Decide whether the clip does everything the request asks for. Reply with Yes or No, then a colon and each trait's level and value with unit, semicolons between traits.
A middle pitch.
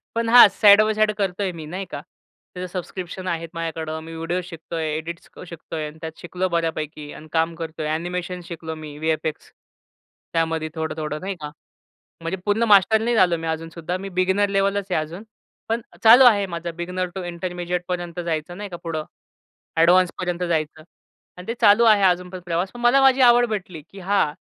Yes: medium, 175 Hz